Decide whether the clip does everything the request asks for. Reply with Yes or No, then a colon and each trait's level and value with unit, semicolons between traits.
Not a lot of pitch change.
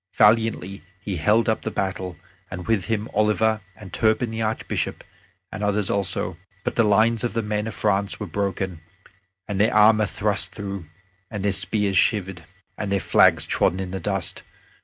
Yes: narrow, 2.2 semitones